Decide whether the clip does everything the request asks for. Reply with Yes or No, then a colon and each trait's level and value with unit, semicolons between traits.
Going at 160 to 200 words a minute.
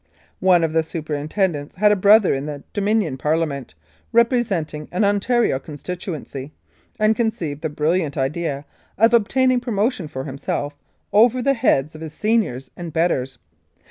No: average, 145 wpm